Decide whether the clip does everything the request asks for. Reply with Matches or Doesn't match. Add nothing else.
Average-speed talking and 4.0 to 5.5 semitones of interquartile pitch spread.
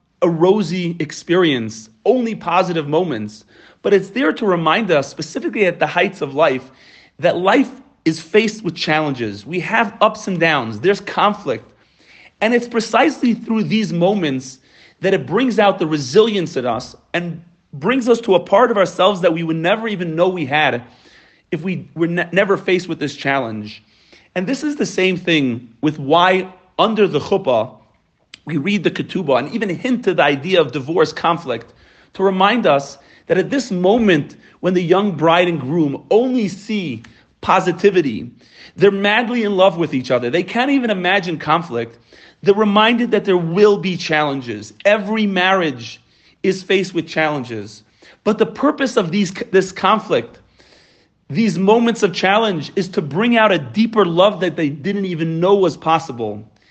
Matches